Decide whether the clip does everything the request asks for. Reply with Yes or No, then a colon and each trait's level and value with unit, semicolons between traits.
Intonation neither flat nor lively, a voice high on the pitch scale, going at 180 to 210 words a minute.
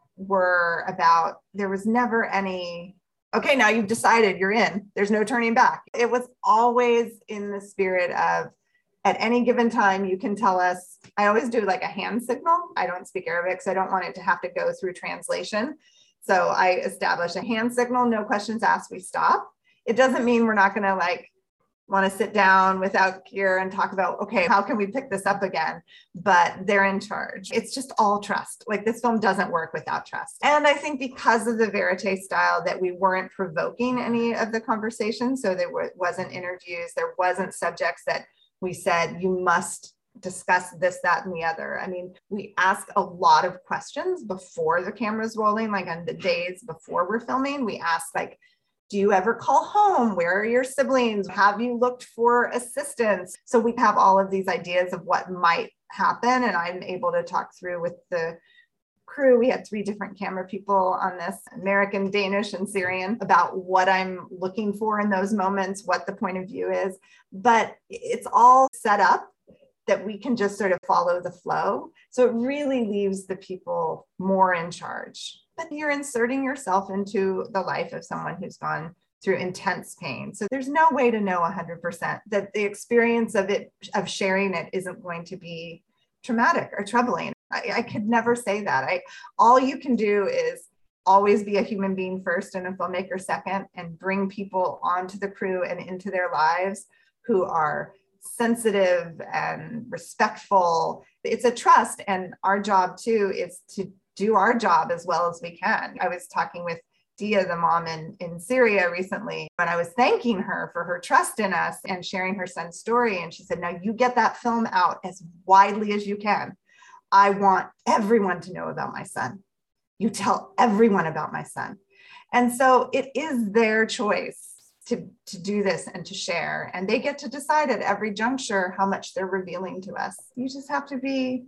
Yes: average, 4.3 semitones; high, 200 Hz; average, 190 wpm